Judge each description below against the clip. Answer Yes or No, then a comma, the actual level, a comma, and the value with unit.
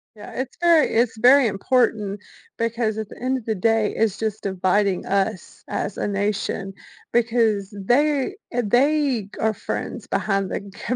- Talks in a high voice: Yes, high, 220 Hz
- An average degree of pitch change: Yes, average, 3.6 semitones